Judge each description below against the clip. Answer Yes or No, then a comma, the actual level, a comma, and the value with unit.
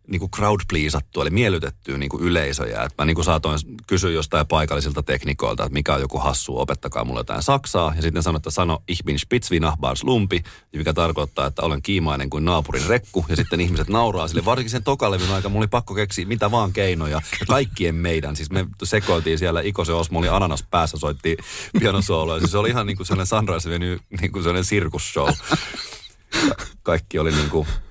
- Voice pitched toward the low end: Yes, very low, 85 Hz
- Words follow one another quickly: Yes, fast, 190 wpm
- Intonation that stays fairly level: No, average, 4.2 semitones